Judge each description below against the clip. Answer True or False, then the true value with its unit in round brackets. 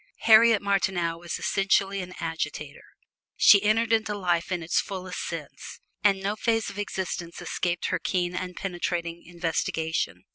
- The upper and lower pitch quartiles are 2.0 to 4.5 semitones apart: True (2.9 semitones)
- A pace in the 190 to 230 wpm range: False (145 wpm)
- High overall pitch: False (180 Hz)